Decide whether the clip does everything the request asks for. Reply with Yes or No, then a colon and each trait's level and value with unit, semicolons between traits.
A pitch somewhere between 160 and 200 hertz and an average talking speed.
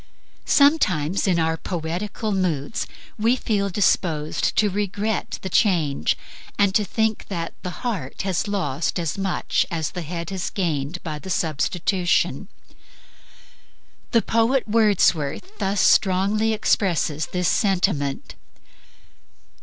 No: medium, 185 Hz; slow, 115 wpm